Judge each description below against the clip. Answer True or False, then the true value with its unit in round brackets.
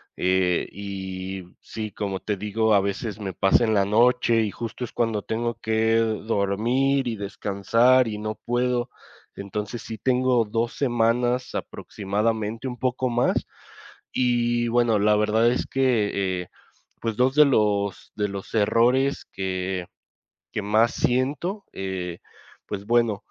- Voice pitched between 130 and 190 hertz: False (110 Hz)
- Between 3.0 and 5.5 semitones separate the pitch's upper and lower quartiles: True (3.3 semitones)